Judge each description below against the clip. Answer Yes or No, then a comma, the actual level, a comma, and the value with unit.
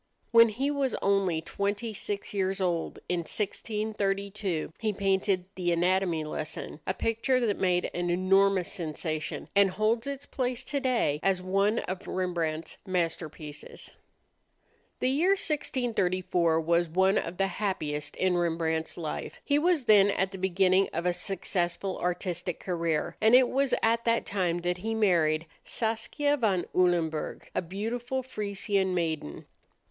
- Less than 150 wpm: Yes, average, 140 wpm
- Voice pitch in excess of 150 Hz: Yes, high, 190 Hz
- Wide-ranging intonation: No, average, 4.0 semitones